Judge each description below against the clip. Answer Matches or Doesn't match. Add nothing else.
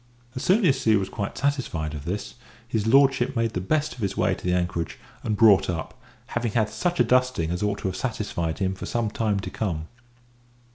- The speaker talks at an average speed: Doesn't match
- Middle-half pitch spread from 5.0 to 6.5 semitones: Matches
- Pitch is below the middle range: Matches